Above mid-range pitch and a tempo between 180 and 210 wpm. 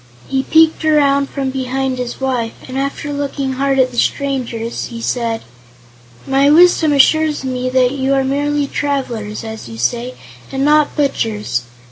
No: very high, 270 Hz; average, 155 wpm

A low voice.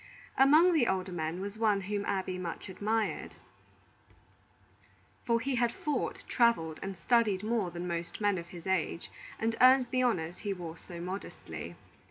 No: high, 200 Hz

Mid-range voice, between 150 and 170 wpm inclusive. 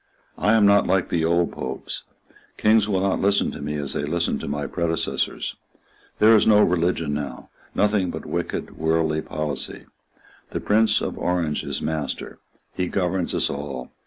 No: very low, 85 Hz; average, 165 wpm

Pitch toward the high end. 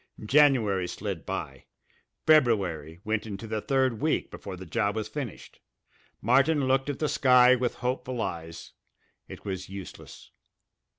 No: low, 115 Hz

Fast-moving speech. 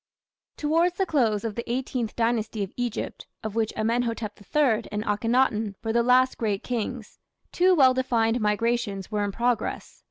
No: average, 160 wpm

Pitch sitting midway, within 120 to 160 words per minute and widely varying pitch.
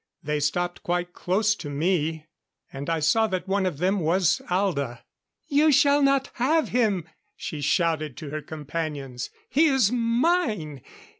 Yes: medium, 180 Hz; average, 150 wpm; wide, 7.2 semitones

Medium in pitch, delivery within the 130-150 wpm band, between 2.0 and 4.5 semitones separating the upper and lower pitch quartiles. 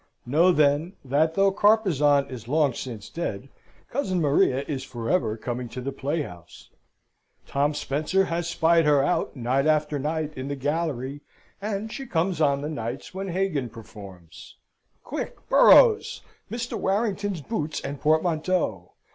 No: medium, 150 Hz; average, 145 wpm; average, 5.1 semitones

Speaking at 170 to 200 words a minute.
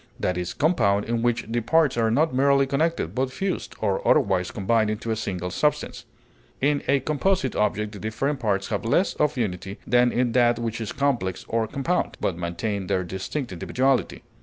Yes: average, 185 wpm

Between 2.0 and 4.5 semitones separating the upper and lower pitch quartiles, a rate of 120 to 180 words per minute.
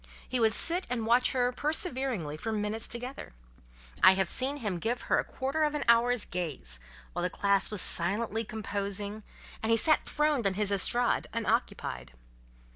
Yes: average, 4.2 semitones; average, 170 wpm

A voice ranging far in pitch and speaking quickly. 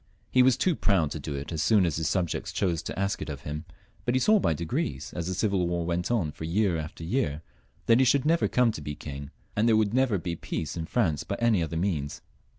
Yes: wide, 6.1 semitones; fast, 255 wpm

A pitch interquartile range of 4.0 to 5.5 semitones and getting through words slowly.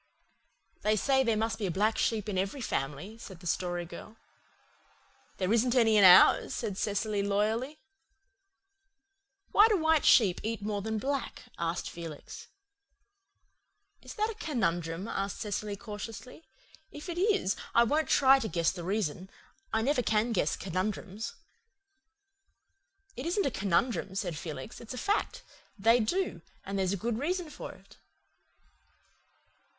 No: average, 5.0 semitones; average, 145 wpm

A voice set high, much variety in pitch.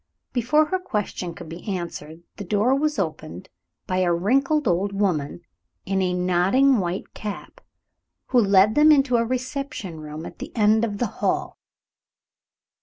Yes: high, 205 Hz; wide, 6.3 semitones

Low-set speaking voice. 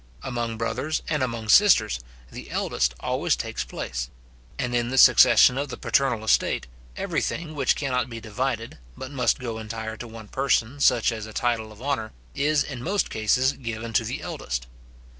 Yes: low, 120 Hz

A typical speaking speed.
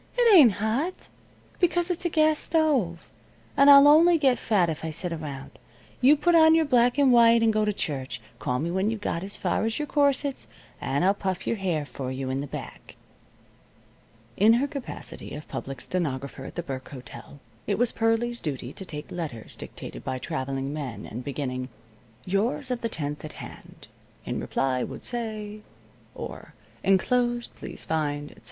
Yes: average, 185 wpm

